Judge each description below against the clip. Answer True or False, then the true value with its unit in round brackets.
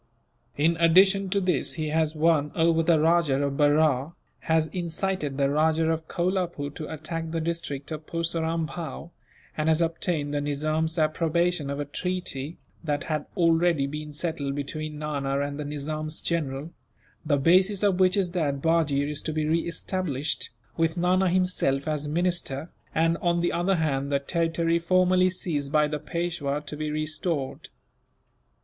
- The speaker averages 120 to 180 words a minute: True (160 wpm)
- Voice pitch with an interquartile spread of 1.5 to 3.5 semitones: True (2.6 semitones)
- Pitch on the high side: False (160 Hz)